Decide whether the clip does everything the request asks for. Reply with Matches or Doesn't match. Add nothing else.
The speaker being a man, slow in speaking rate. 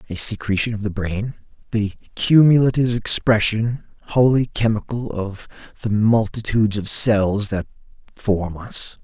Matches